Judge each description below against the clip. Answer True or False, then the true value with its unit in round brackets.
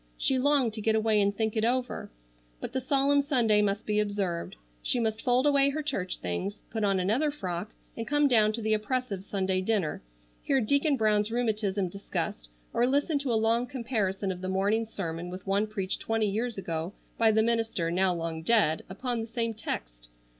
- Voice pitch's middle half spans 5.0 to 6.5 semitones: False (4.0 semitones)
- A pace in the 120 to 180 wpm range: False (195 wpm)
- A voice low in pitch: False (215 Hz)